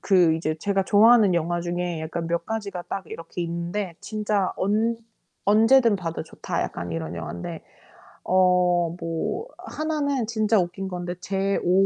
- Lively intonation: No, average, 3.8 semitones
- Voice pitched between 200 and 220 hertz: No, medium, 185 Hz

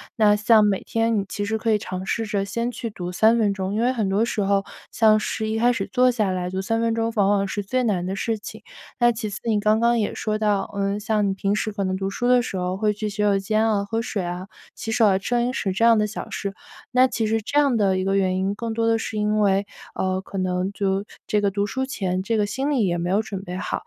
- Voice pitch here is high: Yes, high, 210 Hz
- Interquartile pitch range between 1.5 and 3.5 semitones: Yes, narrow, 2.6 semitones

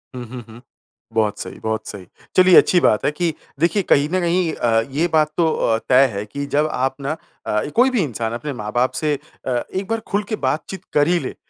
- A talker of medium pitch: Yes, medium, 145 Hz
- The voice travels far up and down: Yes, wide, 6.6 semitones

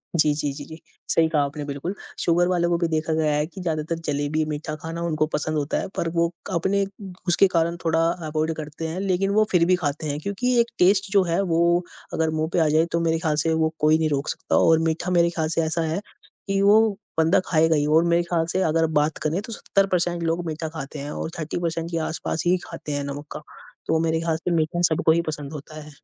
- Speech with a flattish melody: Yes, narrow, 1.9 semitones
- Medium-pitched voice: Yes, medium, 160 Hz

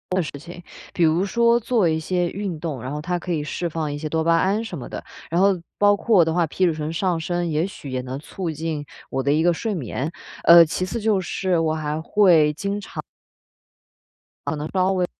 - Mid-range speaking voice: Yes, medium, 170 Hz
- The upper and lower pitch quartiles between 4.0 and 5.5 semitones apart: No, average, 3.3 semitones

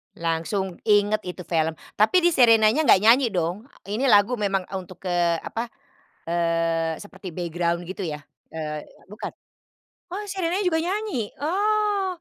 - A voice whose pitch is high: Yes, high, 205 Hz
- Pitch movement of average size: No, wide, 8.5 semitones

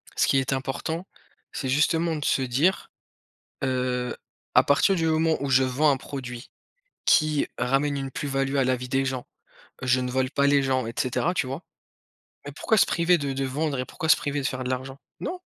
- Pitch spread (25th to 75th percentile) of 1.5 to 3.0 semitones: Yes, narrow, 2.6 semitones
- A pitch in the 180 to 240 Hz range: No, low, 135 Hz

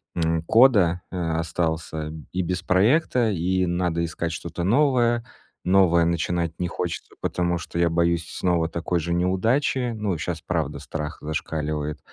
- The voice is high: No, very low, 85 Hz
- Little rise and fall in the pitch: Yes, narrow, 2.2 semitones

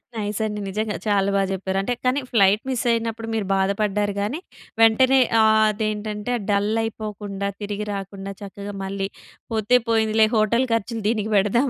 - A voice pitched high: Yes, high, 210 Hz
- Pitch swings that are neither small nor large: No, narrow, 2.0 semitones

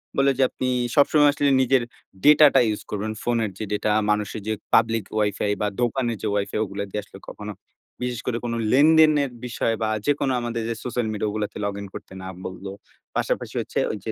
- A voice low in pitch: Yes, low, 115 Hz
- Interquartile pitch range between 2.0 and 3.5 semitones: No, average, 4.0 semitones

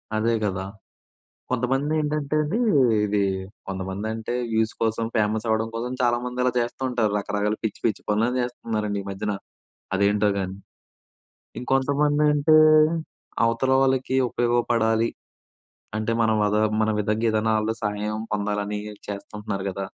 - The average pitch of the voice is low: Yes, low, 110 Hz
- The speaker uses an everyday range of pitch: Yes, average, 3.0 semitones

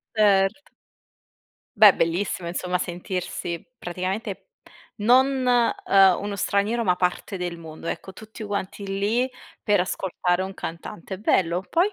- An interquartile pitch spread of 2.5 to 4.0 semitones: Yes, average, 2.8 semitones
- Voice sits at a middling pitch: No, high, 195 Hz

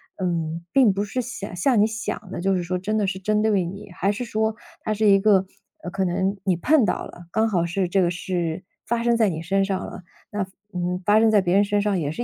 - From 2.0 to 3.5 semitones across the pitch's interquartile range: Yes, average, 3.0 semitones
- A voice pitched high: Yes, high, 195 Hz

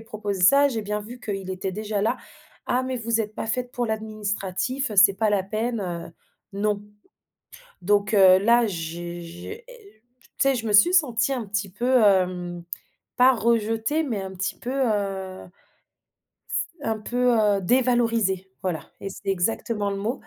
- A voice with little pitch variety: No, average, 3.7 semitones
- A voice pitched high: Yes, high, 210 Hz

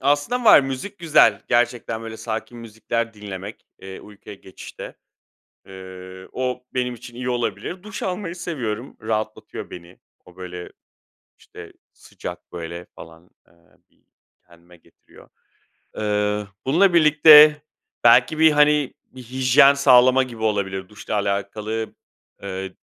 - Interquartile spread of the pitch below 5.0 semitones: No, wide, 5.6 semitones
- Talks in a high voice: No, low, 115 Hz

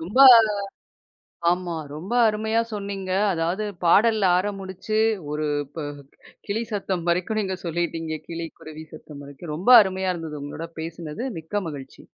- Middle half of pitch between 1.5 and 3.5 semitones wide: No, average, 3.9 semitones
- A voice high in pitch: No, medium, 175 Hz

